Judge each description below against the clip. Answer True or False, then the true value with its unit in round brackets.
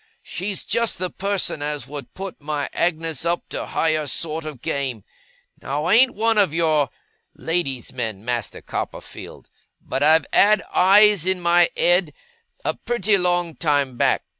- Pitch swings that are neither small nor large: True (4.5 semitones)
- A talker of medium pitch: True (165 Hz)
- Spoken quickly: False (155 wpm)